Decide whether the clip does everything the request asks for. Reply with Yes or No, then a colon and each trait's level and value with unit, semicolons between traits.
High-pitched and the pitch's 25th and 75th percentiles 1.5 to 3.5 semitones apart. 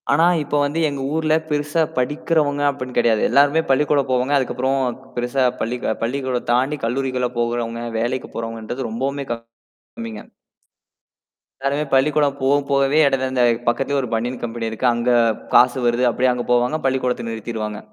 No: low, 130 Hz; average, 2.8 semitones